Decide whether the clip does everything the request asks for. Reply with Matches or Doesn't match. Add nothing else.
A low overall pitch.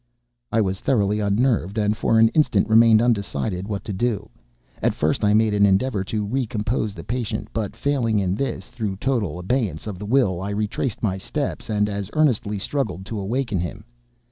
Matches